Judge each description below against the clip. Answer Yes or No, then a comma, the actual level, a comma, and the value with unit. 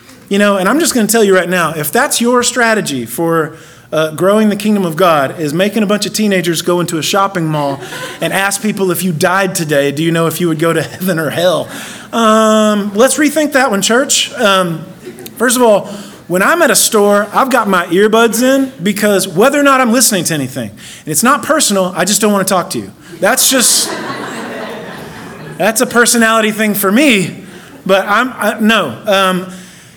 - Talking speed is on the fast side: Yes, fast, 210 wpm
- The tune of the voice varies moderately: Yes, average, 4.4 semitones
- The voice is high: Yes, high, 195 Hz